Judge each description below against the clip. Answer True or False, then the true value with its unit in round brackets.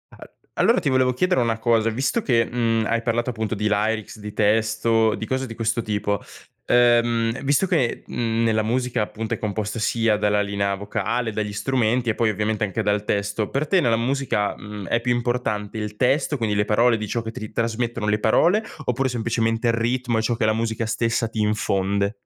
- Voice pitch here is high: False (115 Hz)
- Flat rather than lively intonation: True (2.2 semitones)